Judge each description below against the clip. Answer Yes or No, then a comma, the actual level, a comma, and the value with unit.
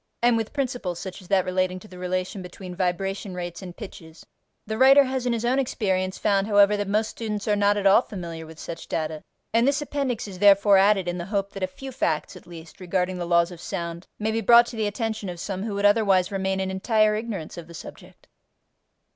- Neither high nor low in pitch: No, high, 195 Hz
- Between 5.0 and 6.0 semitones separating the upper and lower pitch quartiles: No, average, 3.3 semitones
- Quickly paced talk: Yes, fast, 230 wpm